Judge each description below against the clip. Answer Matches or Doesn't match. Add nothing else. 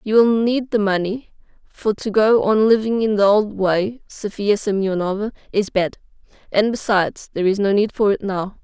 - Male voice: Doesn't match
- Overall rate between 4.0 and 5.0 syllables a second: Matches